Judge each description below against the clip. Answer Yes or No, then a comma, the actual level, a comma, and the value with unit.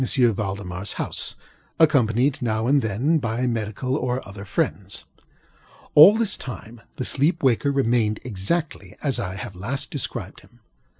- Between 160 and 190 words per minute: No, slow, 135 wpm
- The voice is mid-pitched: No, low, 120 Hz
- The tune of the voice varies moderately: Yes, average, 4.8 semitones